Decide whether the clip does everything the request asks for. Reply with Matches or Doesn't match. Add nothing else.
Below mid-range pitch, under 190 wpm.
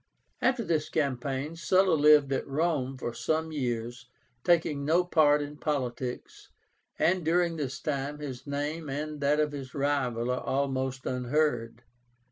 Doesn't match